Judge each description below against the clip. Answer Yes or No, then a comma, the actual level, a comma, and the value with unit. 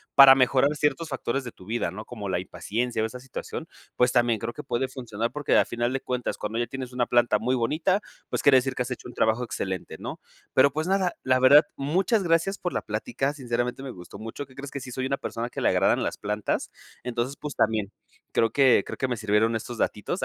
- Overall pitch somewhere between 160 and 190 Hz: No, low, 125 Hz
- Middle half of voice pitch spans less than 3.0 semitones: No, average, 3.3 semitones